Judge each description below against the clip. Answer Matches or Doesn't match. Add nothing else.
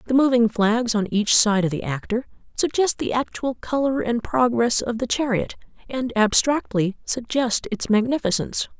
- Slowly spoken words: Doesn't match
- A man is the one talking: Doesn't match